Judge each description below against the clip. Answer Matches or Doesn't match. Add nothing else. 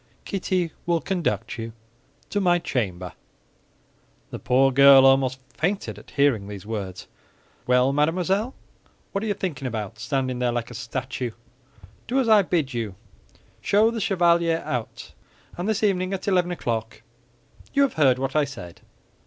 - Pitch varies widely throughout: Matches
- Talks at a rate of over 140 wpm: Matches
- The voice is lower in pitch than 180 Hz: Matches